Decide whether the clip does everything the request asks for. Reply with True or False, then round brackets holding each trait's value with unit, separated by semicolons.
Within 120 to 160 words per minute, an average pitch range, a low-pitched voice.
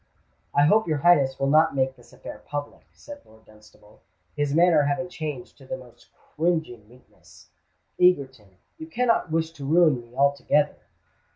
False (155 wpm; 4.2 semitones; 145 Hz)